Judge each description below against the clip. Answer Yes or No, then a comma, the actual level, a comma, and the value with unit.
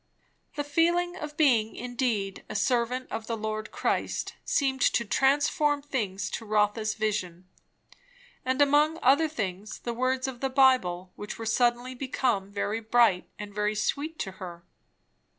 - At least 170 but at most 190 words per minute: No, average, 150 wpm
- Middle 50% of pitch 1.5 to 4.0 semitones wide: No, average, 4.4 semitones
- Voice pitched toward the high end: Yes, high, 240 Hz